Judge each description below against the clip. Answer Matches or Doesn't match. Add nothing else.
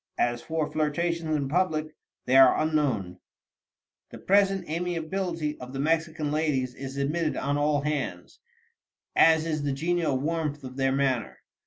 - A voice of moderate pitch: Matches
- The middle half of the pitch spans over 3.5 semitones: Doesn't match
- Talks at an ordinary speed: Matches